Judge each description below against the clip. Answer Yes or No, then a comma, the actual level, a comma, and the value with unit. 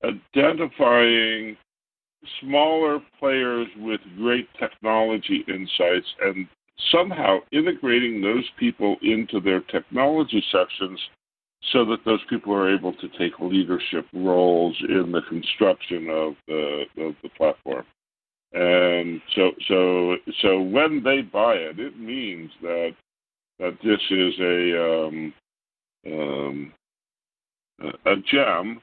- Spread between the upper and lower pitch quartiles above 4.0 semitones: Yes, average, 5.3 semitones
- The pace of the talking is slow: Yes, slow, 110 wpm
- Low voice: Yes, very low, 95 Hz